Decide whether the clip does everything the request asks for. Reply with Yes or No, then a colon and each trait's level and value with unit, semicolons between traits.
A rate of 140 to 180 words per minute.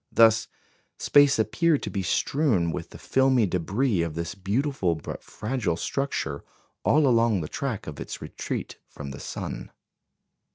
Yes: average, 150 wpm